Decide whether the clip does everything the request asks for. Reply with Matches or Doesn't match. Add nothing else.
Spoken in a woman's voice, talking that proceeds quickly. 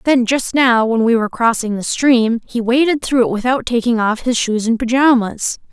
Matches